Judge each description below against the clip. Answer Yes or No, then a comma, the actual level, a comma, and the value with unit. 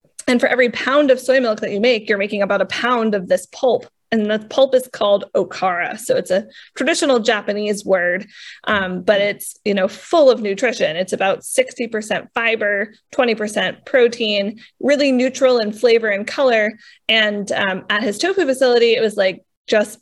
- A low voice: No, high, 220 Hz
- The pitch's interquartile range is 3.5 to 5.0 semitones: Yes, average, 3.9 semitones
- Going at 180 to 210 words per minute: Yes, average, 185 wpm